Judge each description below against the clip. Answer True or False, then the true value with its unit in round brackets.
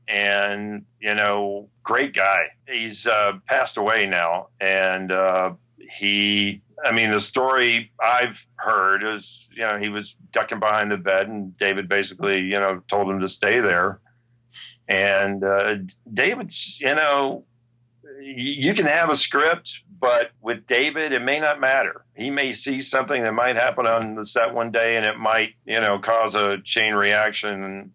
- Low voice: True (105 Hz)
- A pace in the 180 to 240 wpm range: False (165 wpm)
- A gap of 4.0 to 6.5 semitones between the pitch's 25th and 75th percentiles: False (3.2 semitones)